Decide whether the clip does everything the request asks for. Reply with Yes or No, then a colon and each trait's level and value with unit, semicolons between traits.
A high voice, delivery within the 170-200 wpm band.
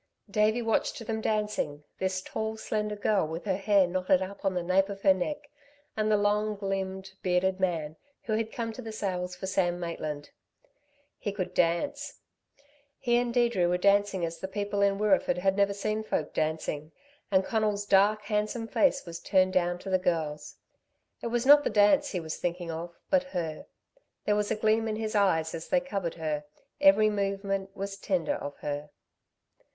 Yes: high, 195 Hz; average, 185 wpm